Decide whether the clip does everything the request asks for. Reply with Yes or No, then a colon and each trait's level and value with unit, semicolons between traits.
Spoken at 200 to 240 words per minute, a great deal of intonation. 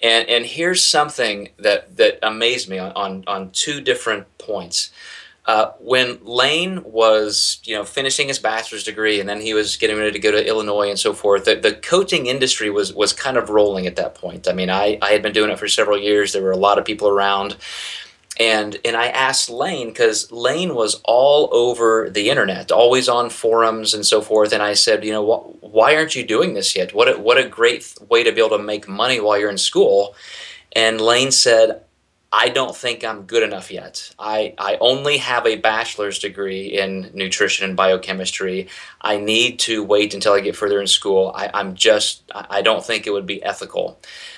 Yes: fast, 205 wpm; wide, 6.1 semitones